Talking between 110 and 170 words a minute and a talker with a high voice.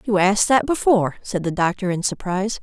No: fast, 205 wpm; high, 195 Hz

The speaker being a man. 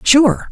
No: female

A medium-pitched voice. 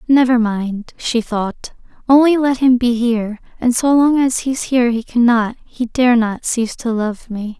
No: high, 240 Hz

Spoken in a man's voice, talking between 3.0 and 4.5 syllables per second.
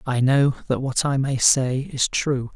Yes: male; 4.0 syllables/s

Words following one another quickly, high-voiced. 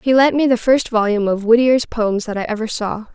Yes: fast, 250 wpm; high, 230 Hz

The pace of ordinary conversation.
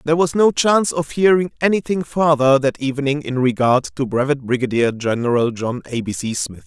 Yes: average, 190 wpm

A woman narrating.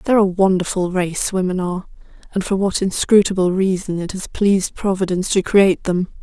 Yes: female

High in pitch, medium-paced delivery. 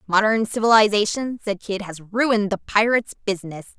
Yes: high, 210 Hz; average, 145 wpm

